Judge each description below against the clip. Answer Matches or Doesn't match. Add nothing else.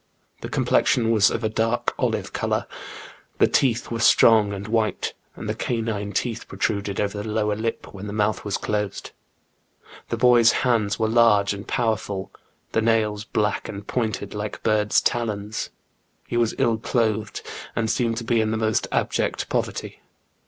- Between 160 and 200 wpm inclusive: Matches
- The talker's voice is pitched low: Matches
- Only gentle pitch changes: Matches